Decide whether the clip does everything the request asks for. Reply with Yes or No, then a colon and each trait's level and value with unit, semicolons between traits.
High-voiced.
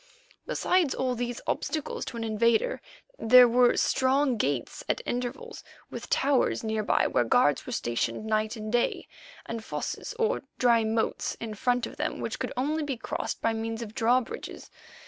Yes: high, 235 Hz